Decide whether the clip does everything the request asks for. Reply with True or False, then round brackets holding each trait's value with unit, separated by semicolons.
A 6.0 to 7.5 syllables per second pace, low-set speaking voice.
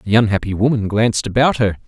True (6.2 syllables/s; 110 Hz)